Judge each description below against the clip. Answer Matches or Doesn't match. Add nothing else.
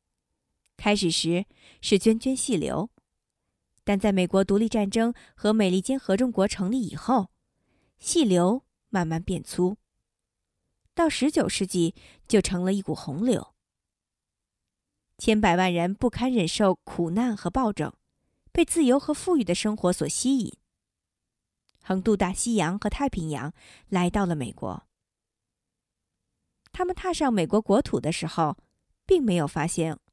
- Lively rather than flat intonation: Matches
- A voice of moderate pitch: Doesn't match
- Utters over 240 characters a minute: Doesn't match